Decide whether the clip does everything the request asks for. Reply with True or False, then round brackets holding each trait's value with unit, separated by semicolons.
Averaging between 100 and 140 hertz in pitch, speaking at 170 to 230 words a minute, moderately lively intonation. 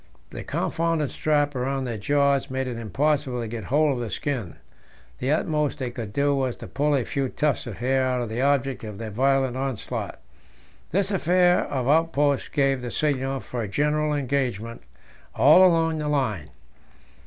True (135 Hz; 175 wpm; 3.3 semitones)